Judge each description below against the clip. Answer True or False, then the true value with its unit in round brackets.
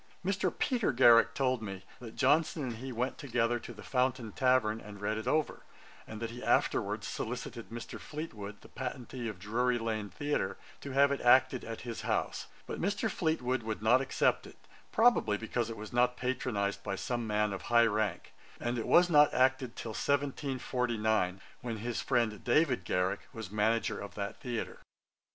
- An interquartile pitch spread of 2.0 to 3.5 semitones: True (3.2 semitones)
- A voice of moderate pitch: False (120 Hz)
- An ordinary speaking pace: True (180 wpm)